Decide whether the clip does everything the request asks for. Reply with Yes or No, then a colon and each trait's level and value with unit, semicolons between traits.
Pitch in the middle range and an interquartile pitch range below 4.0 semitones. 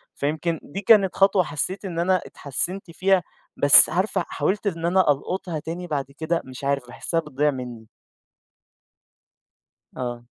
No: medium, 165 Hz; average, 4.8 semitones